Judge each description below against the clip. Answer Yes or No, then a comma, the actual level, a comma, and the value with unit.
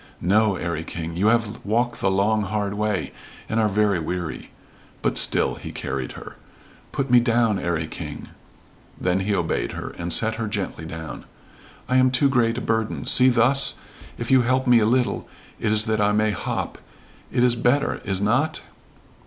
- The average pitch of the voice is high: No, low, 110 Hz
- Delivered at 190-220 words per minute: No, average, 180 wpm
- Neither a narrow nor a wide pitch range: Yes, average, 3.9 semitones